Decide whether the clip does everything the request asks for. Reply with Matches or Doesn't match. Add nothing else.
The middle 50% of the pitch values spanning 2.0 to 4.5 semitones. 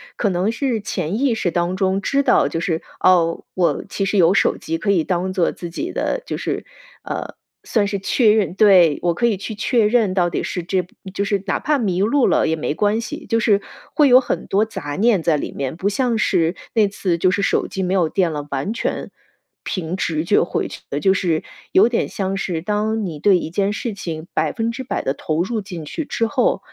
Matches